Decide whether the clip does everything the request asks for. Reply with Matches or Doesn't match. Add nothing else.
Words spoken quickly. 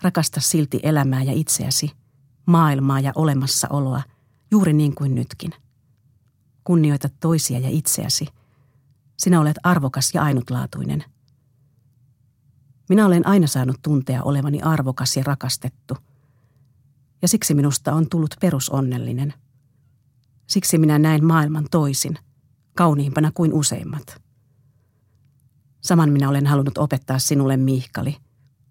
Doesn't match